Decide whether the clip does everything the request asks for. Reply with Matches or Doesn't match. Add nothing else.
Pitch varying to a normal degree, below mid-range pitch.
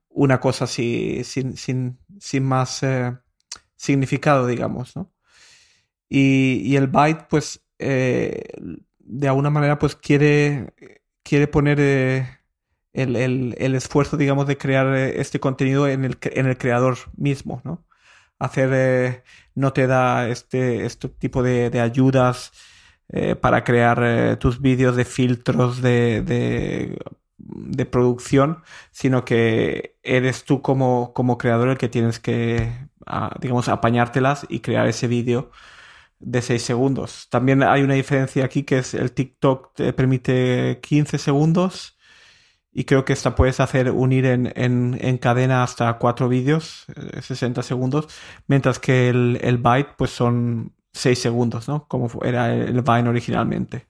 Doesn't match